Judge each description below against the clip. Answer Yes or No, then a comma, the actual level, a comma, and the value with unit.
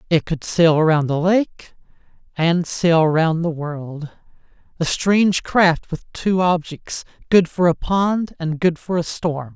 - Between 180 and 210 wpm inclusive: No, average, 155 wpm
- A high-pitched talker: No, medium, 170 Hz